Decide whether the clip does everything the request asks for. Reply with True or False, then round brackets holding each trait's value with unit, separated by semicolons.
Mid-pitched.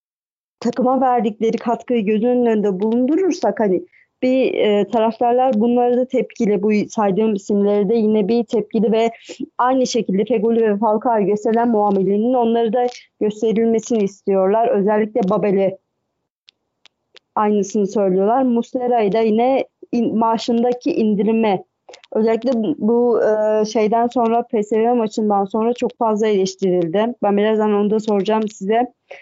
False (225 Hz)